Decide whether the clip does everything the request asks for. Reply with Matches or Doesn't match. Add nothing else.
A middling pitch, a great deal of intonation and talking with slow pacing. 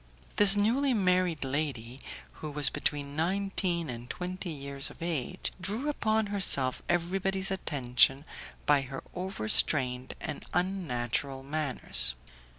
Matches